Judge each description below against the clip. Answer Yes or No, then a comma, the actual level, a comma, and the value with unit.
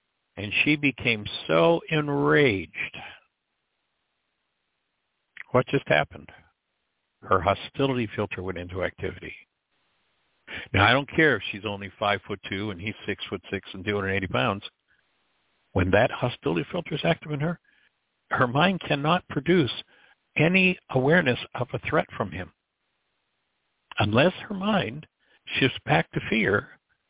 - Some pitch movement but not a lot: No, wide, 7.3 semitones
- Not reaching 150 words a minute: Yes, slow, 135 wpm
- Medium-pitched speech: No, low, 125 Hz